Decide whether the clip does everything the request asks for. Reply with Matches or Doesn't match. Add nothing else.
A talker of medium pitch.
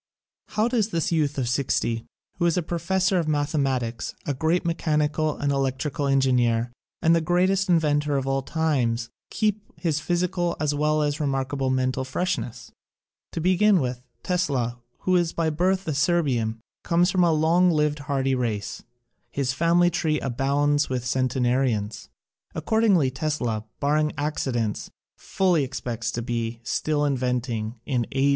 Matches